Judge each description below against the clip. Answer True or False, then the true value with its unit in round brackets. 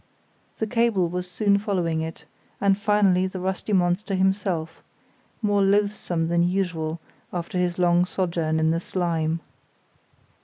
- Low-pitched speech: False (180 Hz)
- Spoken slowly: True (130 wpm)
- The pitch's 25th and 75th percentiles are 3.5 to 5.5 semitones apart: False (2.9 semitones)